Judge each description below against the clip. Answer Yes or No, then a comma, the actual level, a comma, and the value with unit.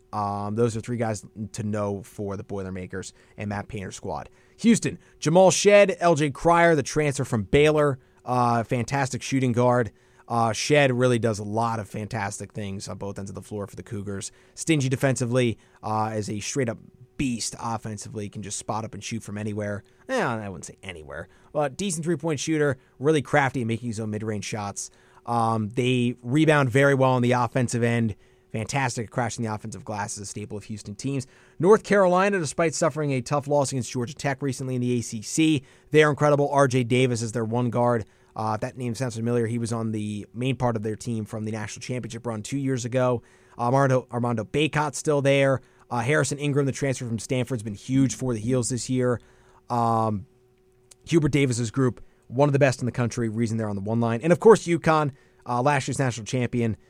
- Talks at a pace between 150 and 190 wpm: No, average, 200 wpm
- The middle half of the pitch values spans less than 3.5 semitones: No, average, 3.8 semitones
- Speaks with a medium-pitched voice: No, low, 125 Hz